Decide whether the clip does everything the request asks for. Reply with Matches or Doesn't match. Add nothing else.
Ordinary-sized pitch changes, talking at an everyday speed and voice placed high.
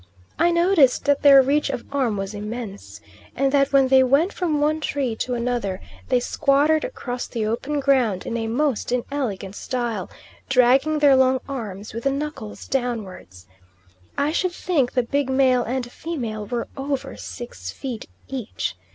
Matches